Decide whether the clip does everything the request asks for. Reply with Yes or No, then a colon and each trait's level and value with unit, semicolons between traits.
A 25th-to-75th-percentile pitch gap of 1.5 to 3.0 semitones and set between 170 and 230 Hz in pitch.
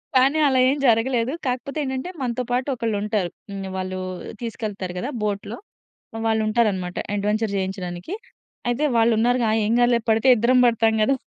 No: average, 3.4 semitones; high, 225 Hz